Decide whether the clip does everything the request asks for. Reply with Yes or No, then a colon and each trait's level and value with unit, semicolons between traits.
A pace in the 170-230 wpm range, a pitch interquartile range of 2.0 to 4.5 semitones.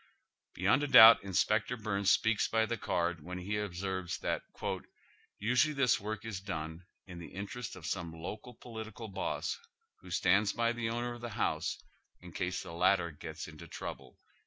Yes: average, 175 wpm; average, 4.1 semitones